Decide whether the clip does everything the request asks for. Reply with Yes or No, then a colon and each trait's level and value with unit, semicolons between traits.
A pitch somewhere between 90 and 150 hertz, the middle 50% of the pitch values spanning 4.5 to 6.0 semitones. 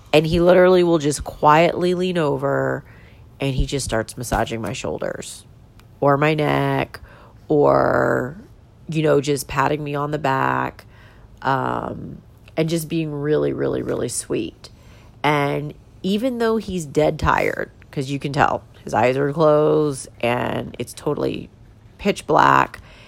Yes: medium, 140 Hz; average, 5.2 semitones